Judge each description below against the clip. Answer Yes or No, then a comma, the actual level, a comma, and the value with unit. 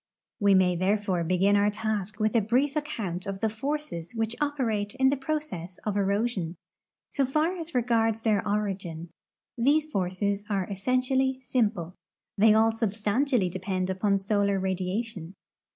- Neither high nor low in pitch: No, high, 210 Hz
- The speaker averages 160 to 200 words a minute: No, average, 150 wpm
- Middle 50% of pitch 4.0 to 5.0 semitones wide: Yes, average, 4.5 semitones